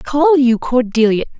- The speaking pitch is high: Yes, very high, 260 Hz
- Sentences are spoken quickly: No, slow, 130 wpm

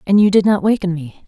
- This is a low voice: No, high, 190 Hz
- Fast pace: Yes, fast, 285 wpm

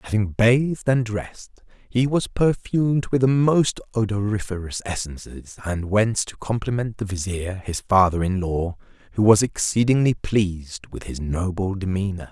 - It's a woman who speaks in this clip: No, male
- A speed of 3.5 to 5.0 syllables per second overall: Yes, 4.6 syllables/s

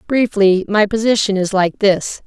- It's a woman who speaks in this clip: Yes, female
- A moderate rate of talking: Yes, average, 160 wpm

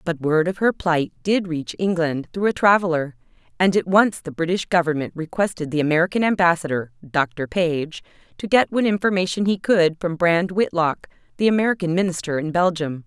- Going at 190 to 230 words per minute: No, average, 170 wpm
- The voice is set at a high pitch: No, medium, 175 Hz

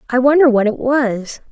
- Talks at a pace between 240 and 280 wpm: No, average, 200 wpm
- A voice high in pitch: Yes, very high, 250 Hz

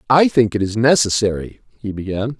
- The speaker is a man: Yes, male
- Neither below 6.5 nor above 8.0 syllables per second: No, 5.1 syllables/s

